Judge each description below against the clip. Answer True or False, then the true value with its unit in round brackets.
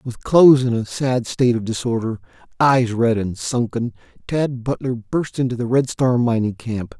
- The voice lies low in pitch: True (120 Hz)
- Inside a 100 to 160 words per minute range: False (180 wpm)